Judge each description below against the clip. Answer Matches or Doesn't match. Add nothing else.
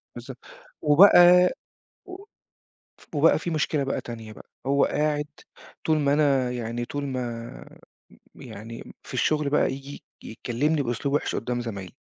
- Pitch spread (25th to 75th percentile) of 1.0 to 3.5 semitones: Doesn't match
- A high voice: Doesn't match